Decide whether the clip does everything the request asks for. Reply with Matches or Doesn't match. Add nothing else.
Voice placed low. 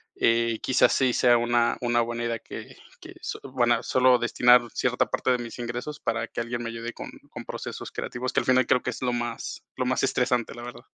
Matches